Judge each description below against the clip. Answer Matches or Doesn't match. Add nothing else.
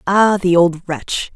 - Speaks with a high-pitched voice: Doesn't match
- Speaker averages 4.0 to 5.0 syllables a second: Doesn't match